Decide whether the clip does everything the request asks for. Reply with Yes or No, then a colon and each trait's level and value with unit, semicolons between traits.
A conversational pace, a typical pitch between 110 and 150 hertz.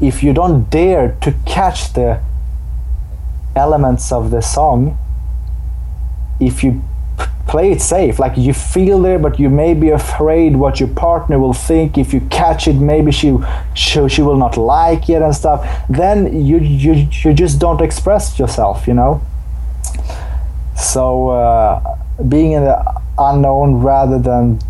Yes: average, 155 wpm; low, 135 Hz